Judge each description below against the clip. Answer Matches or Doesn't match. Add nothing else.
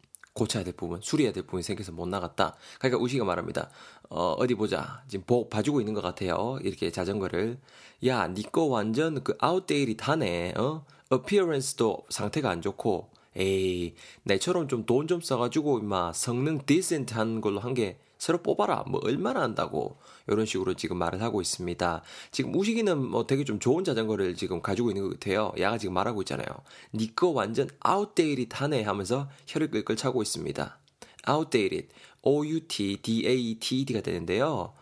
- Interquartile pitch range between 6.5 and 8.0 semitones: Doesn't match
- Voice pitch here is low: Matches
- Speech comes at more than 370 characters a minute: Matches